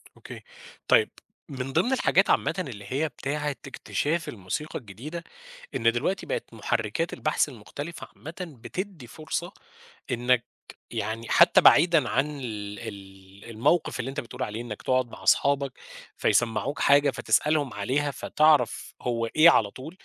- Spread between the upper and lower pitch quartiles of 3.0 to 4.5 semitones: No, average, 5.0 semitones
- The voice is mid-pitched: No, low, 130 Hz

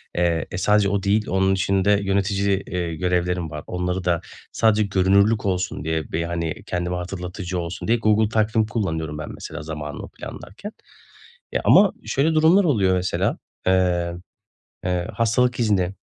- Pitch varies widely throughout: No, average, 3.2 semitones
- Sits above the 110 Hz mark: No, very low, 95 Hz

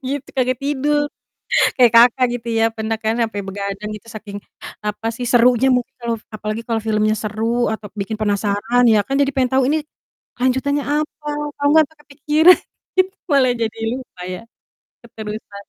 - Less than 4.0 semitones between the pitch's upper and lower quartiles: Yes, average, 3.6 semitones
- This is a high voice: Yes, high, 235 Hz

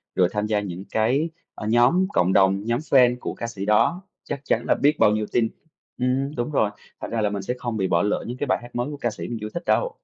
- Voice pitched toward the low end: Yes, low, 115 Hz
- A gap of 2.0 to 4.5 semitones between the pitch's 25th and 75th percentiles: Yes, average, 3.8 semitones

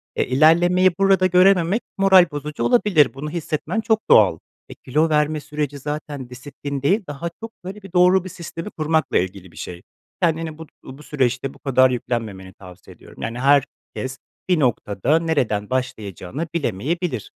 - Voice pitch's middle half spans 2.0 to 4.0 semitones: No, average, 5.3 semitones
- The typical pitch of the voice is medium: Yes, medium, 150 Hz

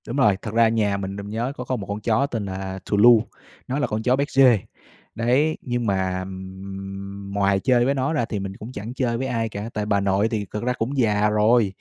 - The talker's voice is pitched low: Yes, low, 110 Hz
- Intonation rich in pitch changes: No, average, 3.7 semitones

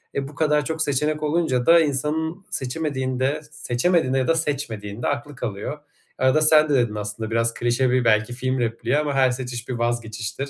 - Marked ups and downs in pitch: No, average, 4.0 semitones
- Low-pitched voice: Yes, low, 130 Hz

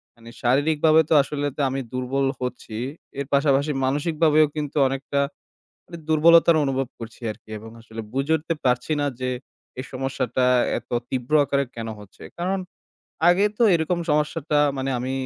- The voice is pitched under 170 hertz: Yes, medium, 140 Hz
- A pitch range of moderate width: Yes, average, 3.4 semitones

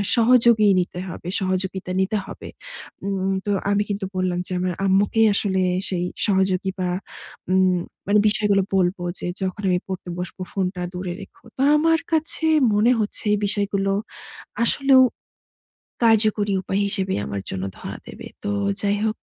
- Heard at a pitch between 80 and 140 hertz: No, high, 195 Hz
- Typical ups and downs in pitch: No, narrow, 2.2 semitones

